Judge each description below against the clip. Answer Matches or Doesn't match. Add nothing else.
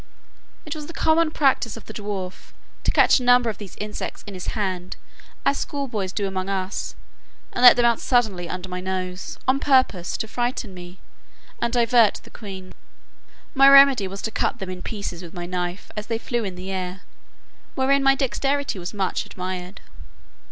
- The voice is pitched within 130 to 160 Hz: Doesn't match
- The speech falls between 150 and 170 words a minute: Doesn't match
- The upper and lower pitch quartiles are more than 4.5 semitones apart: Matches